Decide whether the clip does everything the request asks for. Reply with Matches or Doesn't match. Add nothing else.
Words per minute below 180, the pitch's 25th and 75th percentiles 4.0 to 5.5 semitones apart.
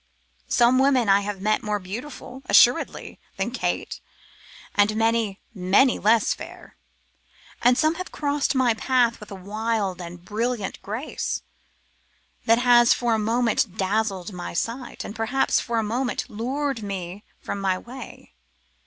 Doesn't match